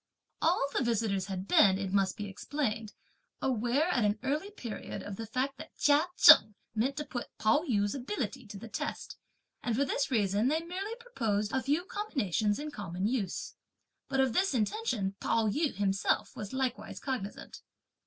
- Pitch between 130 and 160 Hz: No, high, 235 Hz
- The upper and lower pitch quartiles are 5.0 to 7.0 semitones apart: Yes, wide, 5.5 semitones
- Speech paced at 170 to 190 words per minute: Yes, average, 175 wpm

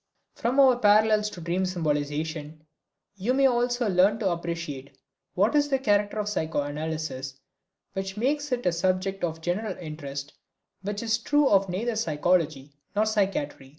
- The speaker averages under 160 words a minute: Yes, average, 150 wpm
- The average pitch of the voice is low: No, high, 190 Hz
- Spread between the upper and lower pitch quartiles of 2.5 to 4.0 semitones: No, wide, 5.5 semitones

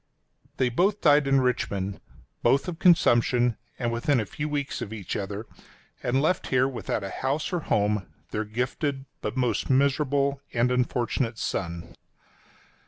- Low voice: Yes, low, 125 Hz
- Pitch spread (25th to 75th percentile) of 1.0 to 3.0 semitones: No, average, 4.0 semitones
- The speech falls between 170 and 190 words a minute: No, average, 155 wpm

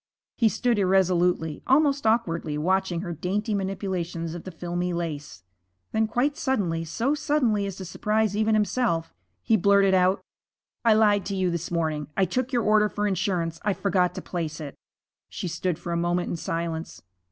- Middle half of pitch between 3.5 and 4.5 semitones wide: Yes, average, 3.9 semitones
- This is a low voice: No, high, 190 Hz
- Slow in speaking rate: No, average, 175 wpm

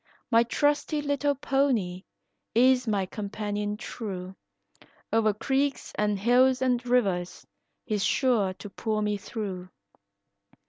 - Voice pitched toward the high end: Yes, high, 220 Hz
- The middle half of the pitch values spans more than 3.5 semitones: Yes, average, 4.2 semitones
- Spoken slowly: Yes, slow, 110 wpm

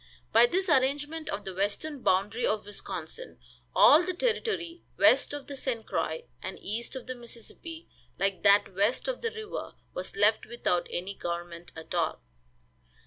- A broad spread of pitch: Yes, wide, 8.4 semitones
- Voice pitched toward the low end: No, high, 240 Hz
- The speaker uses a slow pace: No, average, 160 wpm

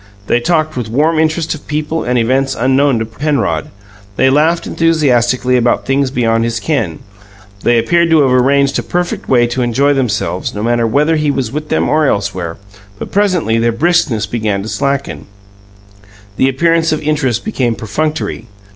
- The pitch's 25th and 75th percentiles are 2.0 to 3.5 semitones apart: No, average, 4.9 semitones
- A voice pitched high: No, low, 135 Hz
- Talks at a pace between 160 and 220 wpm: Yes, average, 170 wpm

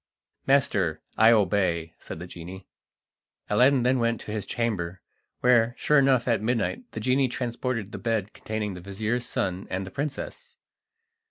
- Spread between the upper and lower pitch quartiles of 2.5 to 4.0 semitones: No, average, 4.4 semitones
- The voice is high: No, low, 110 Hz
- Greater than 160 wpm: No, average, 155 wpm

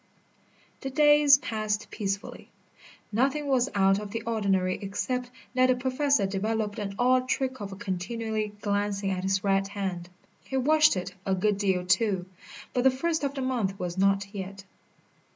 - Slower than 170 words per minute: Yes, average, 160 wpm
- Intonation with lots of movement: No, average, 4.7 semitones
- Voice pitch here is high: Yes, high, 210 Hz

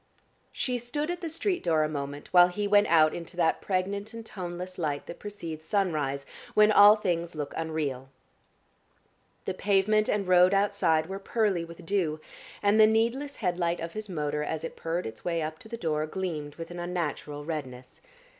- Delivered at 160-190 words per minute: Yes, average, 185 wpm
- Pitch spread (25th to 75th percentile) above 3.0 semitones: Yes, average, 4.6 semitones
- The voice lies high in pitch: No, medium, 175 Hz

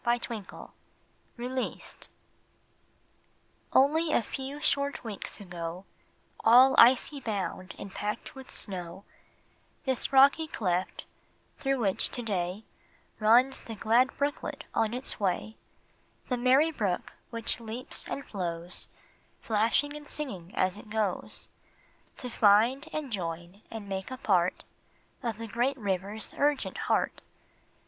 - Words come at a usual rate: No, slow, 125 wpm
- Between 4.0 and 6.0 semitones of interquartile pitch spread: Yes, average, 5.2 semitones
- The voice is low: No, high, 225 Hz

